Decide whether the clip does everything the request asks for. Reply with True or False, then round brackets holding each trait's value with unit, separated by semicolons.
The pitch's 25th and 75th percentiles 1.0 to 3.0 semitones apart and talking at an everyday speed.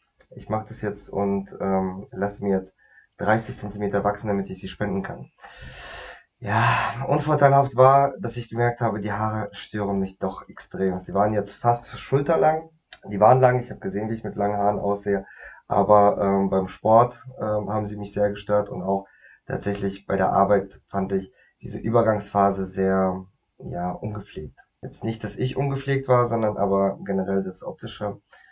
True (2.6 semitones; 170 wpm)